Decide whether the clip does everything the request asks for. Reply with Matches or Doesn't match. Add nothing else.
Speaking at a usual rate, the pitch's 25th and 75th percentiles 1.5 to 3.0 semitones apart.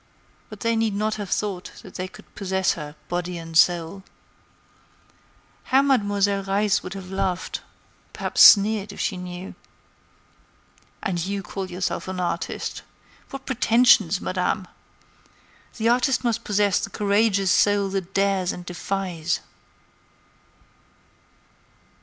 Doesn't match